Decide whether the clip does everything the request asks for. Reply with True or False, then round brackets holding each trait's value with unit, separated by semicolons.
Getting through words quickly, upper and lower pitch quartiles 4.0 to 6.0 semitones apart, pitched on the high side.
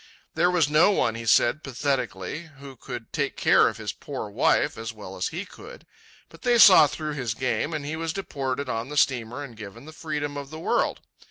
False (210 wpm; 4.9 semitones; 140 Hz)